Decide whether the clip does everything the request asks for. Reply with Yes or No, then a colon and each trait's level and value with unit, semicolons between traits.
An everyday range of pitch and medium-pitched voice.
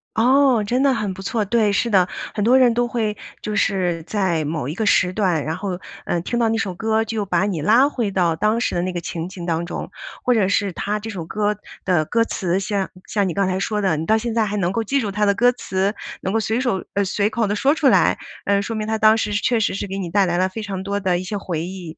No: average, 3.2 semitones; high, 205 Hz